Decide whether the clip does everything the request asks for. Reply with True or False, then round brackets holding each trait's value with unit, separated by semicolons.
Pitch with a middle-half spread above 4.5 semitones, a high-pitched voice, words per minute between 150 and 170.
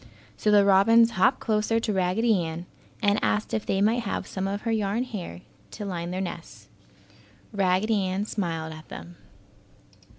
False (3.2 semitones; 200 Hz; 165 wpm)